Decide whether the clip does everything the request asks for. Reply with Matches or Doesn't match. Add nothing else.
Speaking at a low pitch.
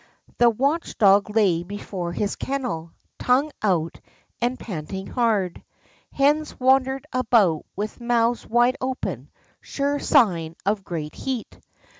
Doesn't match